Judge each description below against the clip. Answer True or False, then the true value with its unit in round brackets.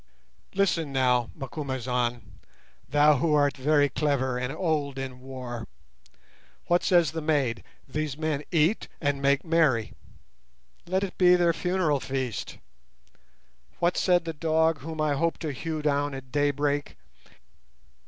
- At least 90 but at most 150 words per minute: True (135 wpm)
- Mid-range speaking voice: True (145 Hz)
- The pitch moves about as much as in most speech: True (3.4 semitones)